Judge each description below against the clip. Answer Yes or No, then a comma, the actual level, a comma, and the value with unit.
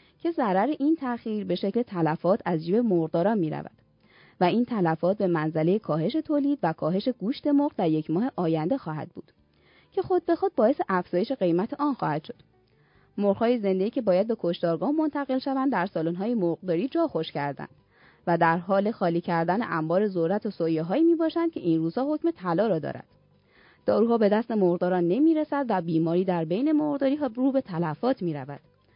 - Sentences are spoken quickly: Yes, fast, 175 wpm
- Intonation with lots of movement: Yes, wide, 8.1 semitones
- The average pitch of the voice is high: Yes, high, 195 Hz